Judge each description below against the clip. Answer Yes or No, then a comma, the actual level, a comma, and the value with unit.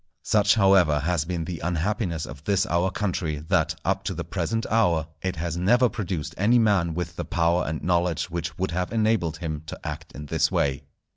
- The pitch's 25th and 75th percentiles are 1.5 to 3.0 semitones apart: No, average, 3.5 semitones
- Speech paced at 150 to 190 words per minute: No, average, 200 wpm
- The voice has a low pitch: Yes, very low, 85 Hz